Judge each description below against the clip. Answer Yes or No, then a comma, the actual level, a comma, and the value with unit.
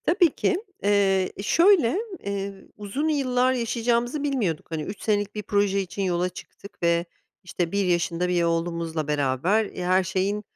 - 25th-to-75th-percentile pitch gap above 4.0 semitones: Yes, average, 5.0 semitones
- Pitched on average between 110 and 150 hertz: No, high, 200 Hz